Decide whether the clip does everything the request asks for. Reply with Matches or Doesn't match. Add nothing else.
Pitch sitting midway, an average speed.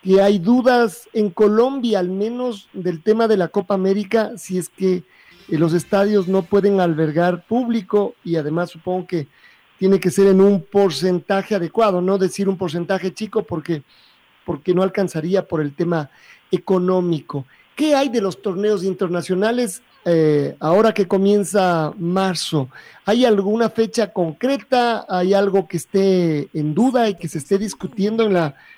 Doesn't match